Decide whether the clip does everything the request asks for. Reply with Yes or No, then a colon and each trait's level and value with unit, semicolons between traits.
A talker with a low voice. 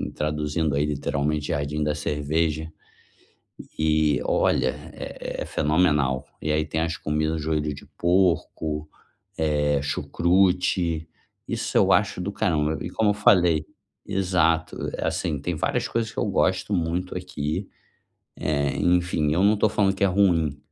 Yes: very low, 80 Hz